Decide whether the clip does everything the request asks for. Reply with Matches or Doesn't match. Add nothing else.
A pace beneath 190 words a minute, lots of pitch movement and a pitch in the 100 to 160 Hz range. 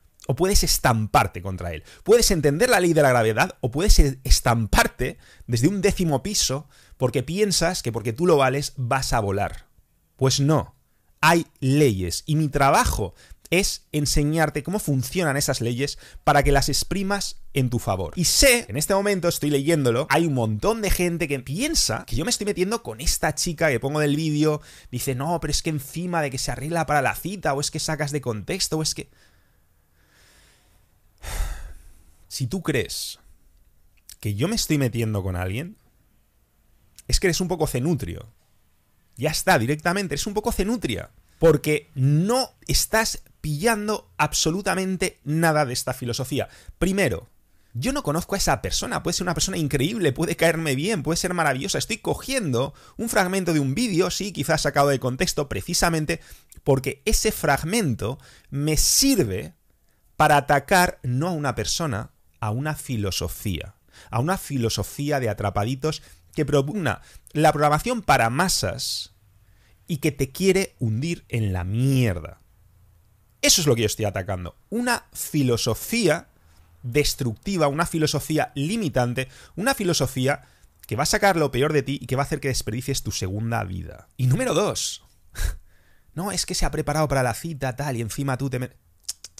Matches